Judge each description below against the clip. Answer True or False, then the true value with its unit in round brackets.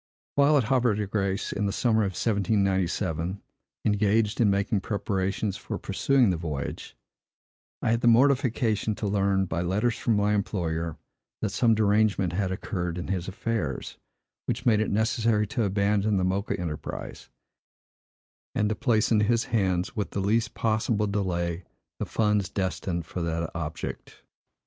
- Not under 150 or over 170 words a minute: True (155 wpm)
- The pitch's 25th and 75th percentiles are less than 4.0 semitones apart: True (2.9 semitones)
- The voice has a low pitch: True (100 Hz)